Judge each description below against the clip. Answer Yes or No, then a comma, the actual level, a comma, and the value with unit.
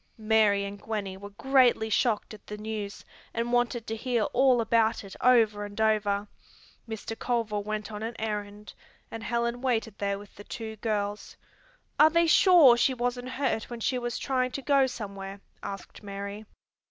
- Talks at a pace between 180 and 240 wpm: No, average, 170 wpm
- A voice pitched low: No, high, 220 Hz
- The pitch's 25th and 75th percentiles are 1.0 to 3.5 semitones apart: Yes, average, 2.9 semitones